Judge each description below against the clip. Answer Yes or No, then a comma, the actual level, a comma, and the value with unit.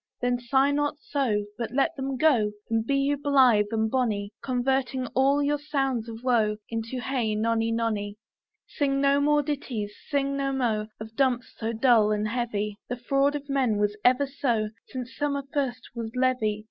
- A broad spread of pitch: No, average, 3.8 semitones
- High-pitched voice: Yes, very high, 250 Hz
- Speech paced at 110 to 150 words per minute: No, average, 175 wpm